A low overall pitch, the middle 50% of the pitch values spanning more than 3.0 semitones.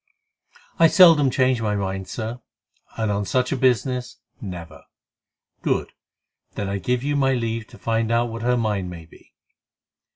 Yes: low, 115 Hz; average, 3.8 semitones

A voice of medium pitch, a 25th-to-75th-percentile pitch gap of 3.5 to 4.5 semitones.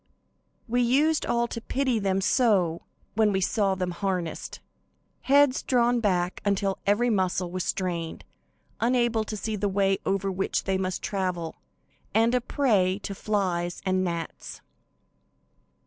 No: high, 195 Hz; average, 4.0 semitones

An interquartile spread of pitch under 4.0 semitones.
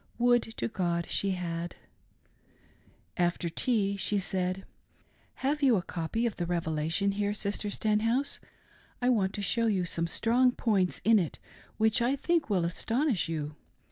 No: average, 4.9 semitones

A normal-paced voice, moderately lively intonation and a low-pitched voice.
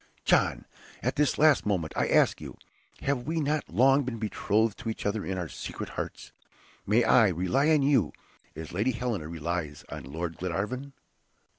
No: average, 170 wpm; wide, 7.2 semitones; low, 110 Hz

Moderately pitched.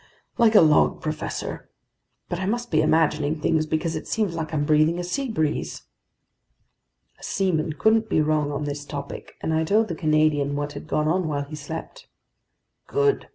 Yes: medium, 155 Hz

